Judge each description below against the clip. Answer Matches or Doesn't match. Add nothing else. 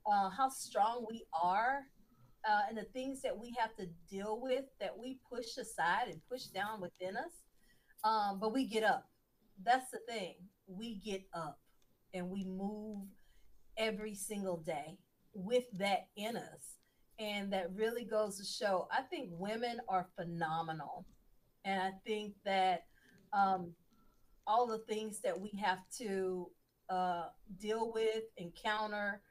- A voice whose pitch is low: Doesn't match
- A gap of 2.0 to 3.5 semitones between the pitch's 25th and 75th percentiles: Matches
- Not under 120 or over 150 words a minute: Matches